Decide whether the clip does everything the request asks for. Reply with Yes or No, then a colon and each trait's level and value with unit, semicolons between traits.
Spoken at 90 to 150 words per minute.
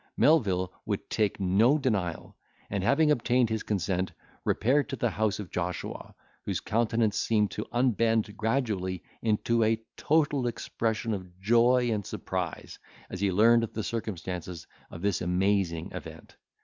Yes: average, 140 wpm